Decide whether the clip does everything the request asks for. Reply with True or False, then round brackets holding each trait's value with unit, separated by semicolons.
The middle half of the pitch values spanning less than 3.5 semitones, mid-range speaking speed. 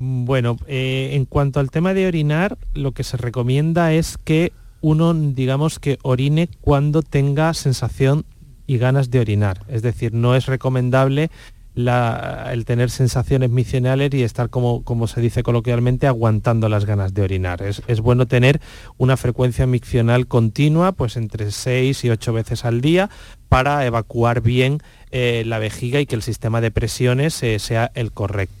True (2.9 semitones; 165 wpm)